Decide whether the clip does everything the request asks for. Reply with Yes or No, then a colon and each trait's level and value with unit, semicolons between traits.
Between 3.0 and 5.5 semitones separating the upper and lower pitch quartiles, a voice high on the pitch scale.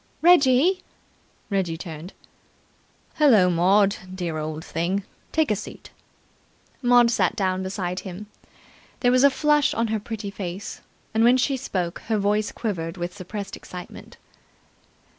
Yes: average, 5.2 semitones; high, 200 Hz